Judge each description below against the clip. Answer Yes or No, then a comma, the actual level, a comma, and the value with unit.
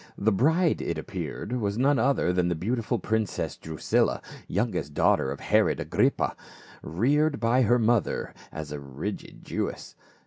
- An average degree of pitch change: No, wide, 6.4 semitones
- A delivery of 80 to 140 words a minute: No, average, 150 wpm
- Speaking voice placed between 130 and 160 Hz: No, low, 110 Hz